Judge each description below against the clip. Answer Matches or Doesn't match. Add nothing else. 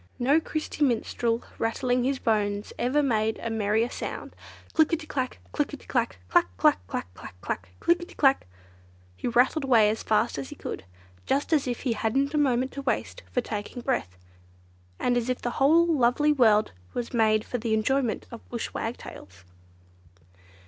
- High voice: Matches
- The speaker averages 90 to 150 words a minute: Doesn't match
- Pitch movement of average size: Matches